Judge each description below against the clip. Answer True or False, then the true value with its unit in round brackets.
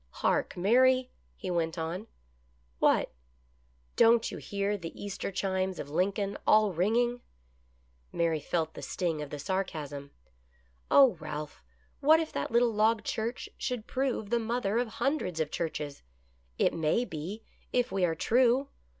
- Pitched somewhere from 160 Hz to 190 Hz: True (185 Hz)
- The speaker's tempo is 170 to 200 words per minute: True (175 wpm)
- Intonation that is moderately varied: False (7.3 semitones)